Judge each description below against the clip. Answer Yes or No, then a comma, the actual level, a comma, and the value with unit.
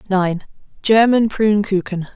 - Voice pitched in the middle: No, high, 200 Hz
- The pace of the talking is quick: No, slow, 85 wpm